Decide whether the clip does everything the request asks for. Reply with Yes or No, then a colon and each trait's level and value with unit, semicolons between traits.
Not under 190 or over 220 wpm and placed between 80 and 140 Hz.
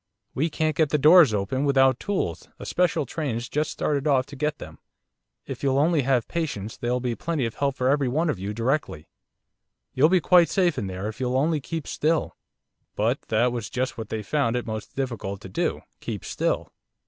Yes: average, 200 wpm; low, 135 Hz